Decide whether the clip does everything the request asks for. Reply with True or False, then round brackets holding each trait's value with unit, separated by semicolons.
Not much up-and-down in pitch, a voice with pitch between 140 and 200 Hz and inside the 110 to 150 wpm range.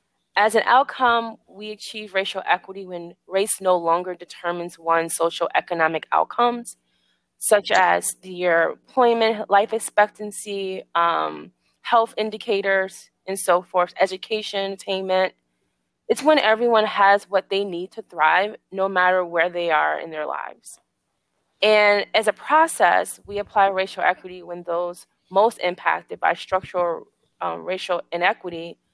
False (3.3 semitones; 190 Hz; 135 wpm)